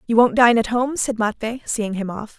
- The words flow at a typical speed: No, fast, 250 wpm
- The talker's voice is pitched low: No, high, 225 Hz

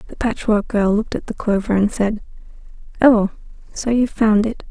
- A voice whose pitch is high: Yes, high, 215 Hz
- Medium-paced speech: Yes, average, 180 wpm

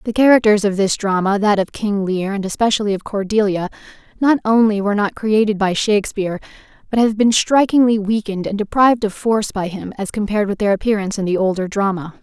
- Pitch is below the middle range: No, high, 205 Hz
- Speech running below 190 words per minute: No, average, 195 wpm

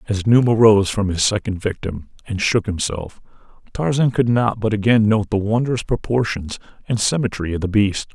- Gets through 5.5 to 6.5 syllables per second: No, 5.0 syllables/s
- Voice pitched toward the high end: No, low, 105 Hz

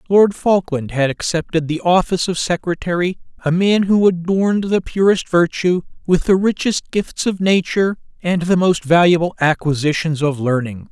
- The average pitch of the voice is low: No, medium, 175 Hz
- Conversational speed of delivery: Yes, average, 155 wpm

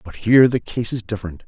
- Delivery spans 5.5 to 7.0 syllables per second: Yes, 6.6 syllables/s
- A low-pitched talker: Yes, low, 110 Hz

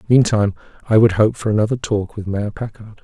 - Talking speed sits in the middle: Yes, average, 195 wpm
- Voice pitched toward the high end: No, low, 105 Hz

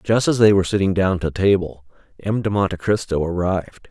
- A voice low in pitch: Yes, very low, 95 Hz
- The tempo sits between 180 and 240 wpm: Yes, average, 200 wpm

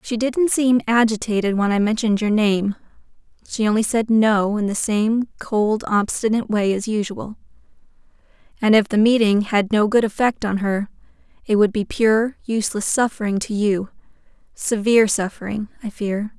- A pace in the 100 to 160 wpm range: Yes, average, 155 wpm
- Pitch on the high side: Yes, high, 215 Hz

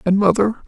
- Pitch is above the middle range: Yes, high, 200 Hz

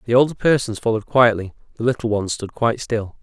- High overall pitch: No, low, 115 Hz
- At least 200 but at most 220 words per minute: Yes, fast, 205 wpm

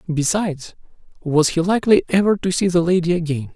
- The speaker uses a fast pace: No, average, 170 wpm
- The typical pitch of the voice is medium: Yes, medium, 175 Hz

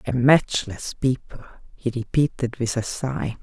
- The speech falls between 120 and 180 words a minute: Yes, average, 140 wpm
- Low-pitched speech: Yes, low, 125 Hz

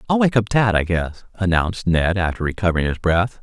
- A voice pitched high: No, very low, 95 Hz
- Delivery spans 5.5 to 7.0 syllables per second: Yes, 5.7 syllables/s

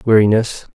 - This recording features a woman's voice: No, male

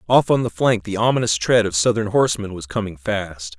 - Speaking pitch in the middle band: No, low, 105 Hz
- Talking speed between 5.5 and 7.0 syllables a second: Yes, 5.6 syllables/s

